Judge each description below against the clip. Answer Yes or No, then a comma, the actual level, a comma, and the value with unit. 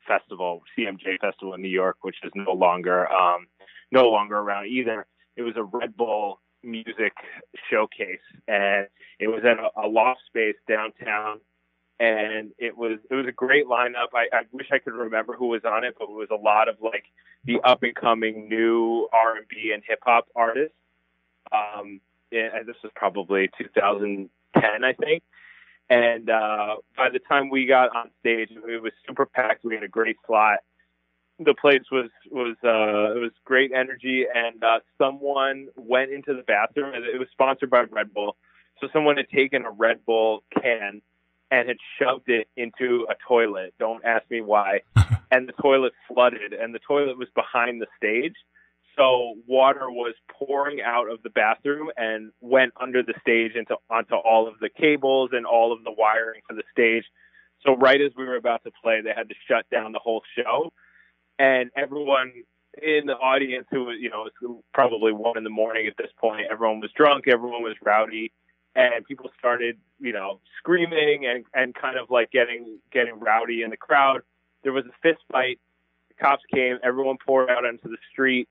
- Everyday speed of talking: Yes, average, 185 wpm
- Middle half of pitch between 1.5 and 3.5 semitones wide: Yes, average, 3.2 semitones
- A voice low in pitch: Yes, low, 115 Hz